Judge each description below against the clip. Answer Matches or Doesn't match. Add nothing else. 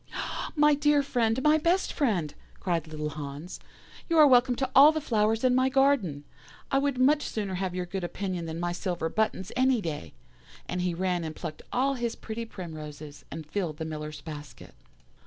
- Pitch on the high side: Matches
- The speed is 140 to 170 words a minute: Doesn't match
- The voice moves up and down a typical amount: Doesn't match